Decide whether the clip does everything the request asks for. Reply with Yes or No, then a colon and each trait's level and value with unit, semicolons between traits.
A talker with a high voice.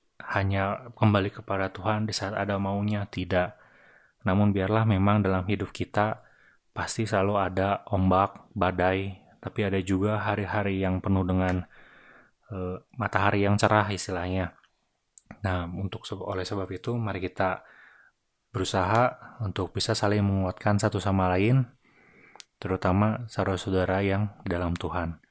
No: low, 100 Hz